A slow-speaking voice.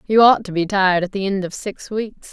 No: fast, 285 wpm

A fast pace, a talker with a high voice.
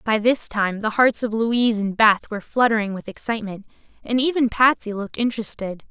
No: average, 185 wpm; high, 220 Hz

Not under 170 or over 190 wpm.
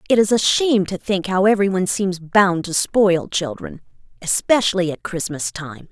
Yes: average, 185 wpm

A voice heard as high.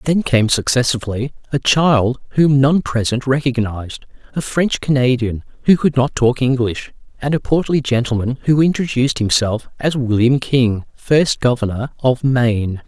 No: low, 130 Hz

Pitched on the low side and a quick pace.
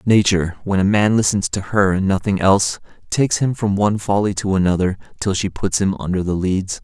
Yes: low, 100 Hz; fast, 210 wpm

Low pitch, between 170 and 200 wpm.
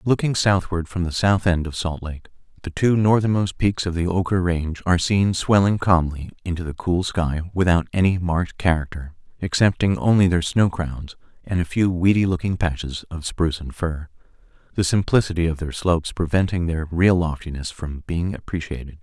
Yes: very low, 90 Hz; average, 175 wpm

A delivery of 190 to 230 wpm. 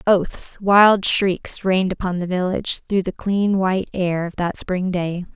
No: average, 180 wpm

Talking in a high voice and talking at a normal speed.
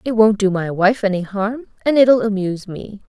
No: high, 205 Hz; fast, 210 wpm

